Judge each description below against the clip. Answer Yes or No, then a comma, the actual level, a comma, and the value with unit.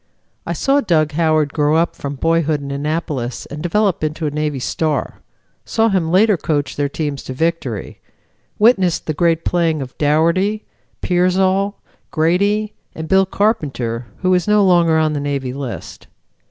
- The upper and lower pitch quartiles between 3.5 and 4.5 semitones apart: Yes, average, 4.2 semitones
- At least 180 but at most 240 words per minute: No, average, 155 wpm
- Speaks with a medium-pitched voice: Yes, medium, 160 Hz